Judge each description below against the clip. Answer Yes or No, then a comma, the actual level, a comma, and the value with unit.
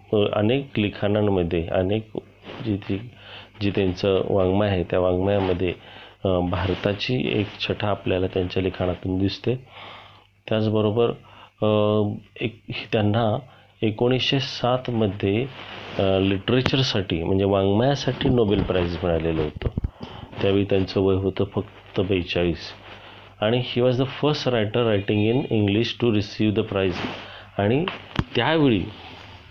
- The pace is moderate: Yes, average, 105 wpm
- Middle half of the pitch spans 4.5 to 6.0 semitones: No, average, 3.3 semitones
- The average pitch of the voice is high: No, low, 100 Hz